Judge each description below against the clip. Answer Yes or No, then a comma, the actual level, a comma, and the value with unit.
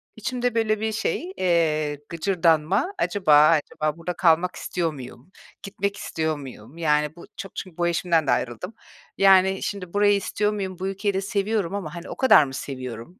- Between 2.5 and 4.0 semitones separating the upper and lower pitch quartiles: No, average, 4.6 semitones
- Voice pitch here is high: No, medium, 180 Hz